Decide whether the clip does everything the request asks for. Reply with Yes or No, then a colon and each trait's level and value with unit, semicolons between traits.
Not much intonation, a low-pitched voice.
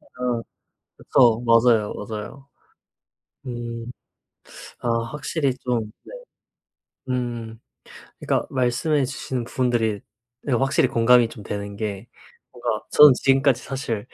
Yes: narrow, 2.3 semitones; low, 120 Hz